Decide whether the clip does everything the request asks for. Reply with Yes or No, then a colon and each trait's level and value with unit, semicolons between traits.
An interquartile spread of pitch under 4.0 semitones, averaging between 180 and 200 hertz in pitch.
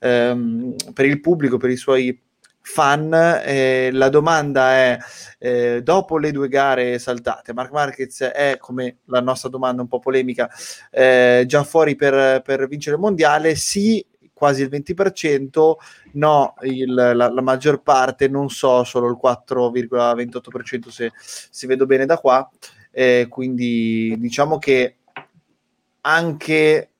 No: narrow, 2.5 semitones; low, 130 Hz